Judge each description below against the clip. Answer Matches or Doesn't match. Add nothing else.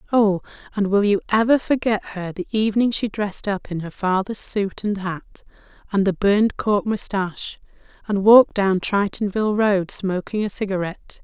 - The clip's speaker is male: Doesn't match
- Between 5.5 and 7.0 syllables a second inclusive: Doesn't match